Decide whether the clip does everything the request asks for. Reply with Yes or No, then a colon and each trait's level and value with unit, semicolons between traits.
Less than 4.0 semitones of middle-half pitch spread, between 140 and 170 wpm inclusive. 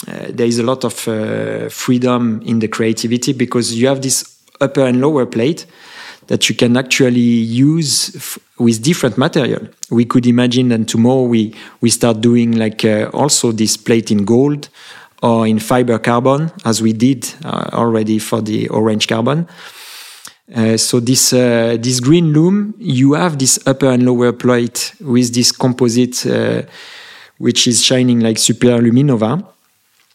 Yes: narrow, 2.4 semitones; average, 160 wpm